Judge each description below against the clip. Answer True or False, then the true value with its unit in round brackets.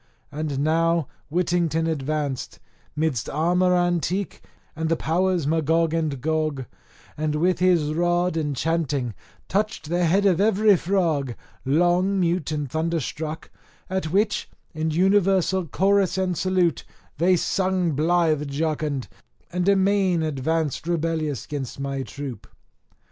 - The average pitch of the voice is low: False (165 Hz)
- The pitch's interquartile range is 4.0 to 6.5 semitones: False (3.0 semitones)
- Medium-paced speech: False (120 wpm)